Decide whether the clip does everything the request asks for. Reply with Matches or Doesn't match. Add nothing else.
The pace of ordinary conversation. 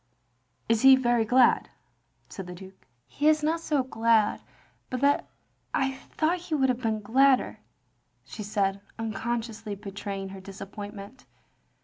Matches